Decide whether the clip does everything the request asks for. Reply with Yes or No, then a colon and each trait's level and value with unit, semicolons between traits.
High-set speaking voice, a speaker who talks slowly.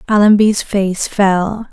Yes: high, 200 Hz; slow, 105 wpm